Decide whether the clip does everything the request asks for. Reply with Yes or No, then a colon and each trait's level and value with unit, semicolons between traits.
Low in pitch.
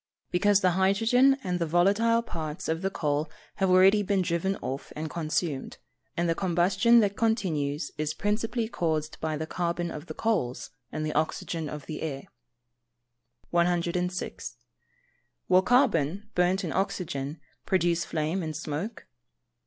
No: medium, 175 Hz